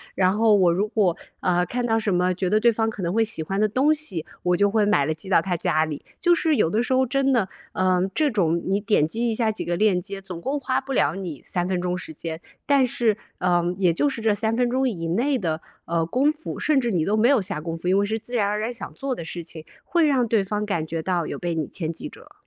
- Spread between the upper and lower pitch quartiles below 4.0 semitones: No, wide, 5.4 semitones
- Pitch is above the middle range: Yes, high, 200 Hz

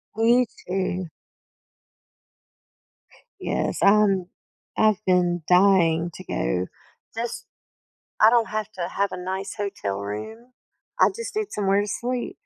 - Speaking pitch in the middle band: No, high, 200 Hz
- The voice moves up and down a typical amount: Yes, average, 3.9 semitones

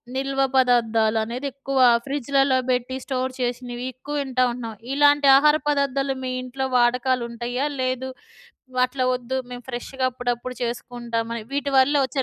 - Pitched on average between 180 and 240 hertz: No, very high, 255 Hz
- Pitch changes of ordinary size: No, narrow, 2.0 semitones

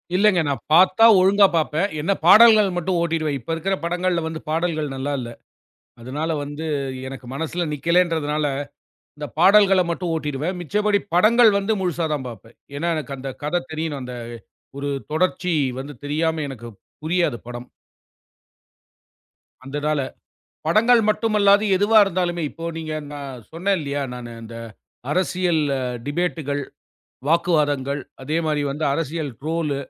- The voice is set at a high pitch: No, medium, 160 Hz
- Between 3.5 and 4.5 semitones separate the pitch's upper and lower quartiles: Yes, average, 4.0 semitones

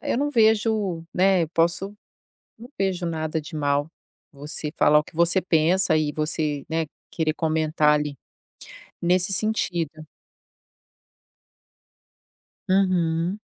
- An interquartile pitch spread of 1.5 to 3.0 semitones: No, average, 3.4 semitones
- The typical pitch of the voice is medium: Yes, medium, 165 Hz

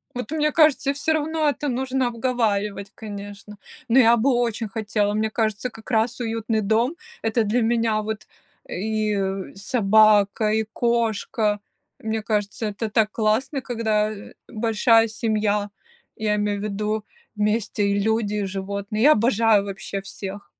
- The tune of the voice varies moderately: No, narrow, 2.1 semitones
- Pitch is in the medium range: No, high, 220 Hz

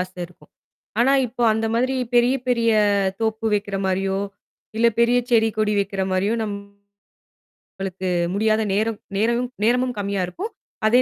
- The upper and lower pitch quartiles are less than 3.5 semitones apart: Yes, average, 2.9 semitones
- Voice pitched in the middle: No, high, 220 Hz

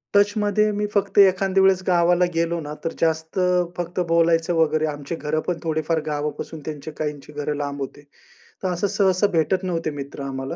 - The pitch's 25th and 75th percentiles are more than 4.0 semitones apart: No, average, 3.5 semitones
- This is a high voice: No, medium, 165 Hz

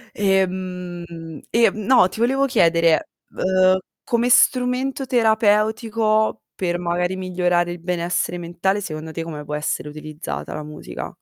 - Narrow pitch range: No, average, 4.4 semitones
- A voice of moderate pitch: Yes, medium, 180 Hz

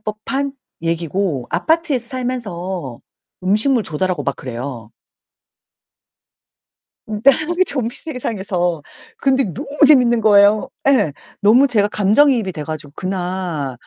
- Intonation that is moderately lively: No, wide, 6.8 semitones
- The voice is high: Yes, high, 200 Hz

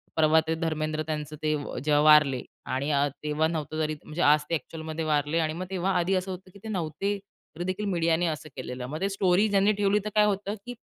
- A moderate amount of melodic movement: Yes, average, 3.7 semitones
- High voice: No, medium, 160 Hz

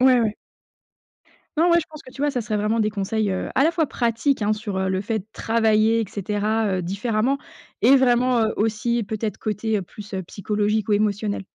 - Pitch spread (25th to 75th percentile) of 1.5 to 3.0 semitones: Yes, narrow, 2.6 semitones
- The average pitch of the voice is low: No, high, 220 Hz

